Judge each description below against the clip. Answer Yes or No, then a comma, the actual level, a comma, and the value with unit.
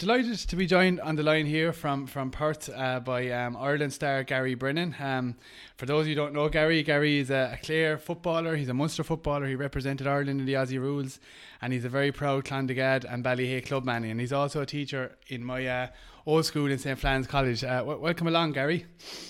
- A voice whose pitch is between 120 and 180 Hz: Yes, medium, 140 Hz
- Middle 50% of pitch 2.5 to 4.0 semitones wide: Yes, average, 2.9 semitones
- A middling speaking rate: No, fast, 225 wpm